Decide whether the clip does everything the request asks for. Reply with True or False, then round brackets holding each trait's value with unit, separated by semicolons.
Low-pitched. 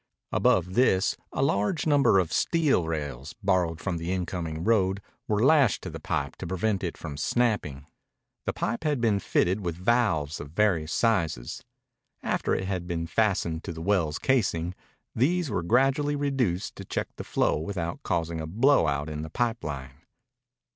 True (95 Hz)